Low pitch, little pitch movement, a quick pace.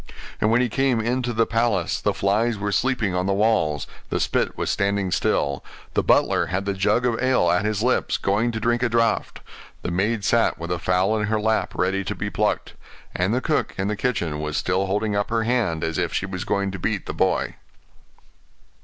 No: low, 105 Hz; average, 3.7 semitones; fast, 215 wpm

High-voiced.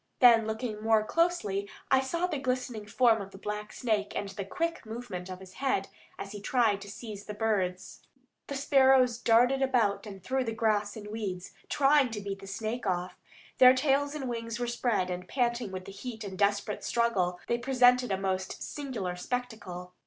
Yes: high, 220 Hz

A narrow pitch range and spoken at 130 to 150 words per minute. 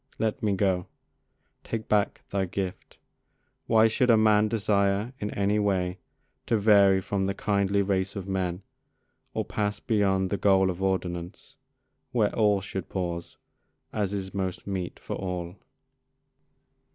Yes: narrow, 1.7 semitones; average, 140 wpm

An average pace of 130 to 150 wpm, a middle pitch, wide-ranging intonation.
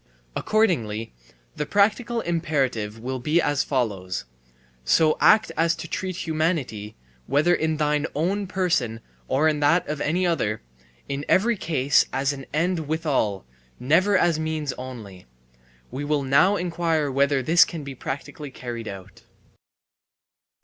No: slow, 135 wpm; medium, 150 Hz; average, 4.6 semitones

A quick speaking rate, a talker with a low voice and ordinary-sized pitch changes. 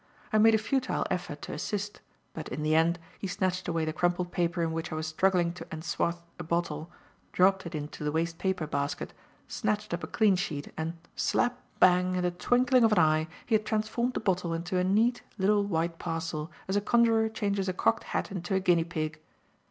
No: fast, 210 wpm; medium, 180 Hz; average, 3.9 semitones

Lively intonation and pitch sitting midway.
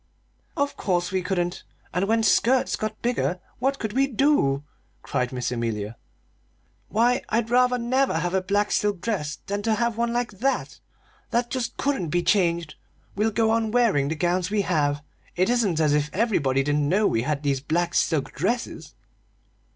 No: wide, 7.2 semitones; high, 200 Hz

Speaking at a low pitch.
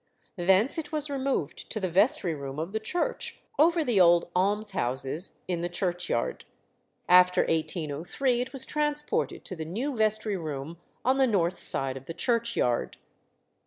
No: high, 190 Hz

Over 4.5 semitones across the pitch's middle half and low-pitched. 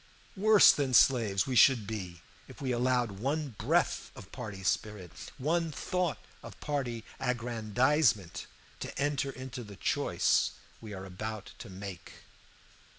Yes: average, 5.1 semitones; low, 120 Hz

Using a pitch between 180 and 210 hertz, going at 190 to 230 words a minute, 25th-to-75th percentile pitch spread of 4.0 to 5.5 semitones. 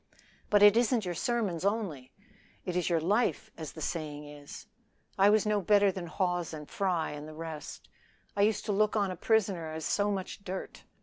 Yes: medium, 185 Hz; average, 195 wpm; average, 4.3 semitones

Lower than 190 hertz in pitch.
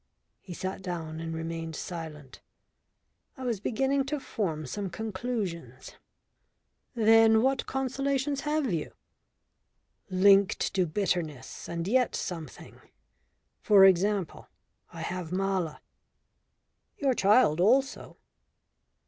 No: high, 195 Hz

